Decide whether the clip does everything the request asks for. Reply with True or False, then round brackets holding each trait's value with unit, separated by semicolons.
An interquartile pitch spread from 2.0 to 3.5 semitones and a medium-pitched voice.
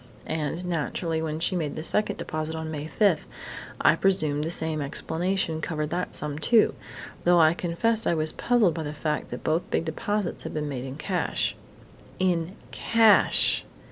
True (2.8 semitones; 160 Hz)